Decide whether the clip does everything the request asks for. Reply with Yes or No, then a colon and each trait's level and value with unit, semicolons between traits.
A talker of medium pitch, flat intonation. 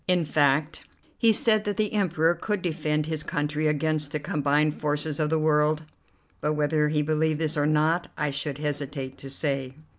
Yes: medium, 150 Hz; narrow, 1.3 semitones